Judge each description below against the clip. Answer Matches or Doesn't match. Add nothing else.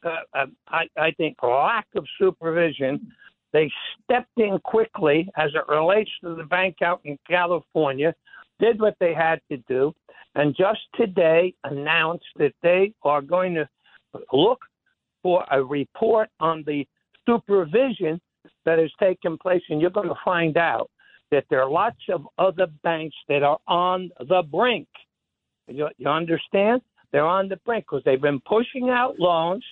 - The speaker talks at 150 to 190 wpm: Matches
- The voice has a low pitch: Doesn't match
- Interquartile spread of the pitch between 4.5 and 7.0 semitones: Matches